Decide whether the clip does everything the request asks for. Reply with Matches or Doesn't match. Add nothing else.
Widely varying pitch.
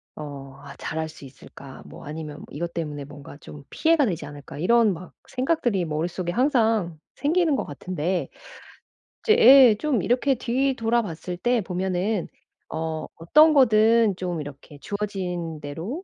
Matches